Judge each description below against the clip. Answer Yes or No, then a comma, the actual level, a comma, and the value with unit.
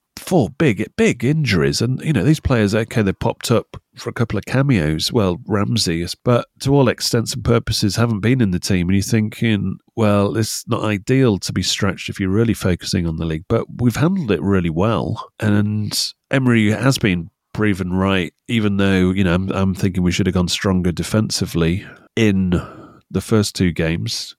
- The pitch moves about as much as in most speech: Yes, average, 3.9 semitones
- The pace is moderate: Yes, average, 190 wpm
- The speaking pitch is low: Yes, low, 105 Hz